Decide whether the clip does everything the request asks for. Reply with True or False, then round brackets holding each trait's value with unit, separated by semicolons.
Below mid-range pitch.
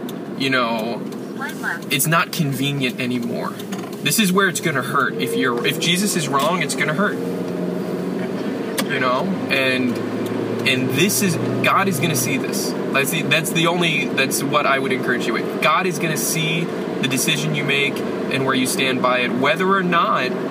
False (165 Hz)